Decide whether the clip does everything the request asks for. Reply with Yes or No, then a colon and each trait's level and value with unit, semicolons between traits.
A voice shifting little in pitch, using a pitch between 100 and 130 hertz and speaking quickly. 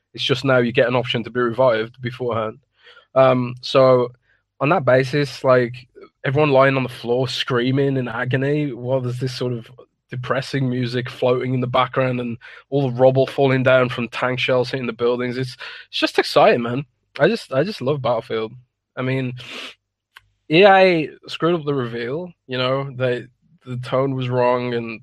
No: narrow, 1.8 semitones; low, 125 Hz; average, 175 wpm